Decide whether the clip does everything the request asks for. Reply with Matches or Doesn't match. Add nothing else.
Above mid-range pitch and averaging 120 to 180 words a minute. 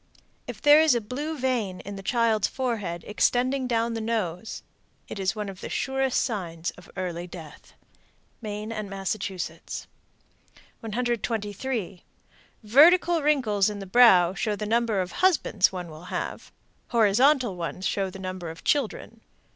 Matches